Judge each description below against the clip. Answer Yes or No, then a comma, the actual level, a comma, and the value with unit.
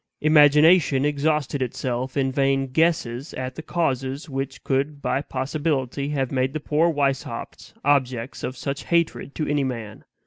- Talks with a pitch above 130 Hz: Yes, medium, 140 Hz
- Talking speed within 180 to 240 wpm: No, average, 145 wpm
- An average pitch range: No, narrow, 2.3 semitones